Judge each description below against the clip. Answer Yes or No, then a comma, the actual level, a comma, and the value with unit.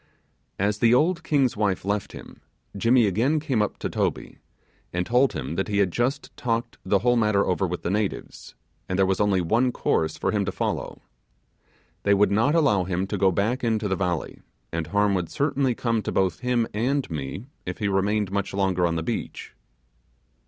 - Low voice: Yes, low, 105 Hz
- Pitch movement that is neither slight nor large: Yes, average, 4.2 semitones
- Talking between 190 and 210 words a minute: Yes, average, 195 wpm